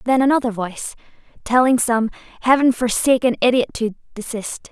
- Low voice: No, high, 240 Hz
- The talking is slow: Yes, slow, 125 wpm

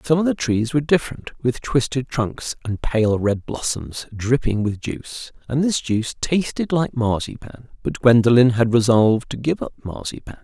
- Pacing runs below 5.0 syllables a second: Yes, 4.8 syllables/s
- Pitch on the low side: Yes, low, 125 Hz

